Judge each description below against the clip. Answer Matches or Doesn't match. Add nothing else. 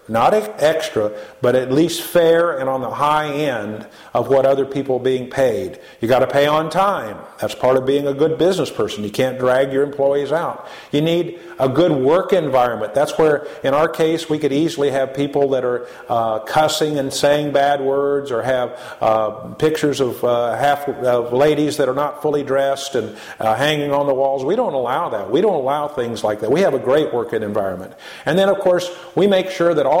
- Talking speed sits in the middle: Doesn't match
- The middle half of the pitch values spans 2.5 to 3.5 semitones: Matches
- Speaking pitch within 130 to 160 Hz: Matches